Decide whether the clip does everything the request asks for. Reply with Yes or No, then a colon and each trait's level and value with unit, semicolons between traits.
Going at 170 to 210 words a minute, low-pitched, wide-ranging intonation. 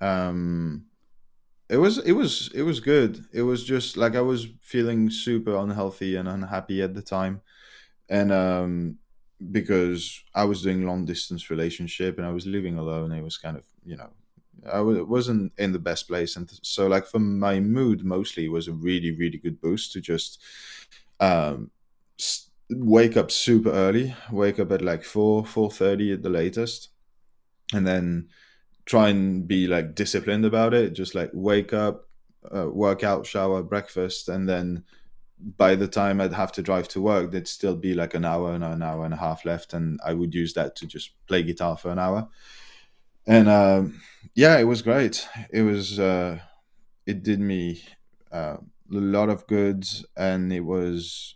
No: average, 180 wpm; very low, 95 Hz; average, 3.2 semitones